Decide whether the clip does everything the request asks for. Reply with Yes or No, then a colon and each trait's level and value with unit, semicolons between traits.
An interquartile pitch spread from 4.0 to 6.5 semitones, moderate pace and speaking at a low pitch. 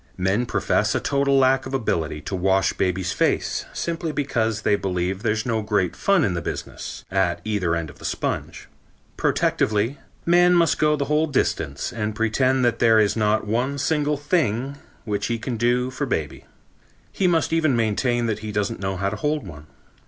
Yes: wide, 5.6 semitones; average, 185 wpm; low, 115 Hz